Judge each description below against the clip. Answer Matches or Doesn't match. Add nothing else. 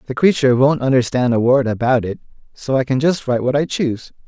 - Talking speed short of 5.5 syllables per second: Doesn't match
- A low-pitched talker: Matches